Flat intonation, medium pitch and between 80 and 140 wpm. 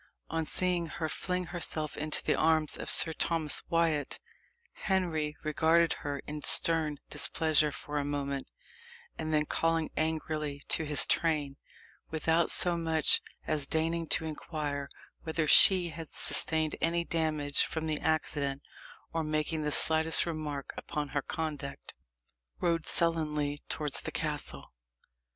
Yes: narrow, 1.7 semitones; medium, 155 Hz; slow, 135 wpm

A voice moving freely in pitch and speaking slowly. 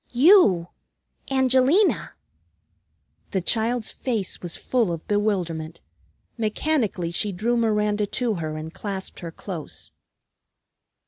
Yes: wide, 5.7 semitones; slow, 105 wpm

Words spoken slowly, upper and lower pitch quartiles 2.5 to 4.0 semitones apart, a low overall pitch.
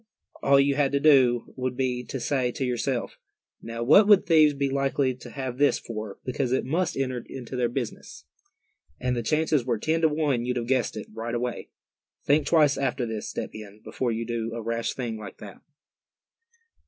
No: average, 195 wpm; average, 3.0 semitones; low, 125 Hz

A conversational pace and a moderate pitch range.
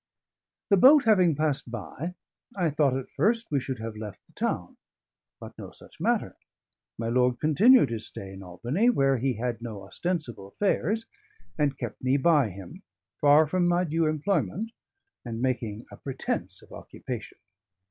No: average, 160 wpm; wide, 7.0 semitones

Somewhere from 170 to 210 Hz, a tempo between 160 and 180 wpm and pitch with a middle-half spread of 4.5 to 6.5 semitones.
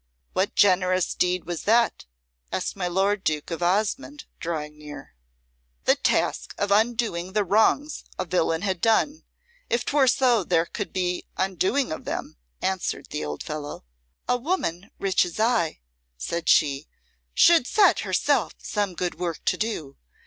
No: medium, 185 Hz; average, 150 wpm; average, 4.8 semitones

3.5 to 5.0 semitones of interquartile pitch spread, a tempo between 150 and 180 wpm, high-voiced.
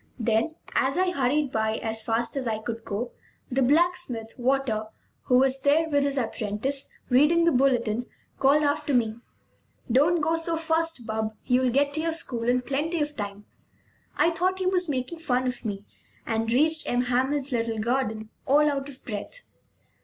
Yes: average, 4.7 semitones; average, 175 wpm; very high, 265 Hz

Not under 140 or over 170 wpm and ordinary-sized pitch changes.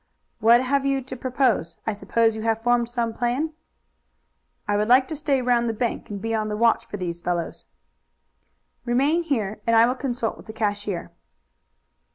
No: average, 185 wpm; average, 3.1 semitones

